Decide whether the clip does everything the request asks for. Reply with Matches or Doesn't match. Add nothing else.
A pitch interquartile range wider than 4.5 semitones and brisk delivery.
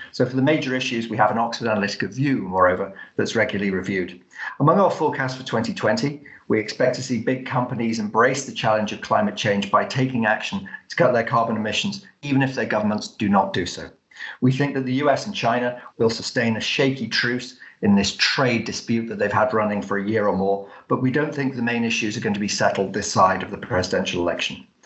Doesn't match